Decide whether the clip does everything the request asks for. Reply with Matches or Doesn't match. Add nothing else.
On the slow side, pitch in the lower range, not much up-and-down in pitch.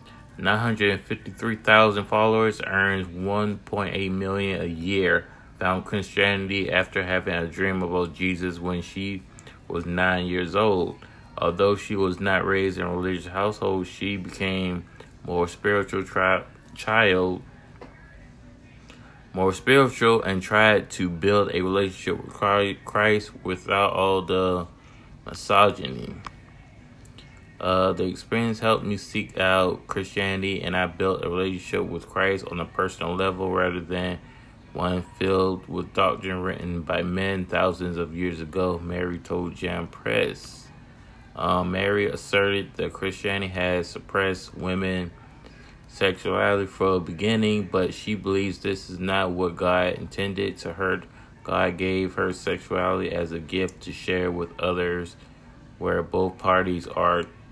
Matches